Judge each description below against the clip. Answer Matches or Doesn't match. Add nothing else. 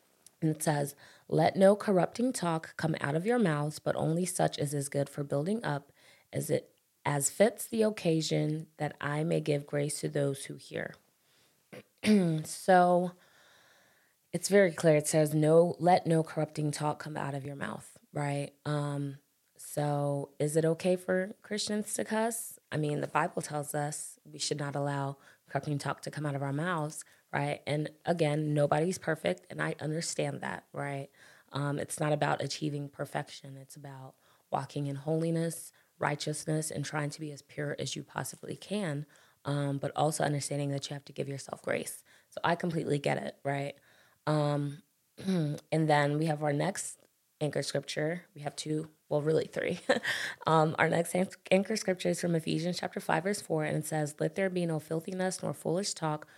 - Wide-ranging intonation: Doesn't match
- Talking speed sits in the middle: Matches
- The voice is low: Doesn't match